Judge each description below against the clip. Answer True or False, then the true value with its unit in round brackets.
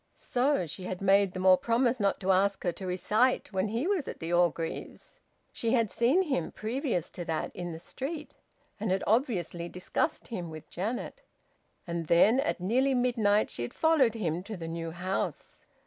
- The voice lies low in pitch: False (200 Hz)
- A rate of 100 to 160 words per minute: False (185 wpm)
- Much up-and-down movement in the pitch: True (5.7 semitones)